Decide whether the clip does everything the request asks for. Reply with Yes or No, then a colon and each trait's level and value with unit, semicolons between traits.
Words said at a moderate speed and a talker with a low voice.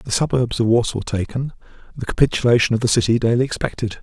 Yes: average, 180 wpm; low, 115 Hz